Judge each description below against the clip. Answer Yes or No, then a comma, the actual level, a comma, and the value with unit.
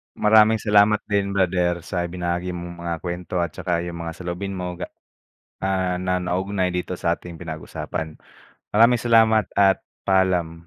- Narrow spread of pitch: Yes, narrow, 2.2 semitones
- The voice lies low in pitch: Yes, very low, 90 Hz